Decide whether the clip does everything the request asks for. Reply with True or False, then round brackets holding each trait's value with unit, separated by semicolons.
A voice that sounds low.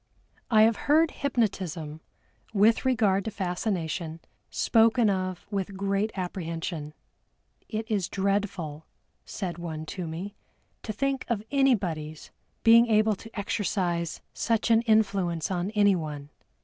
False (195 Hz)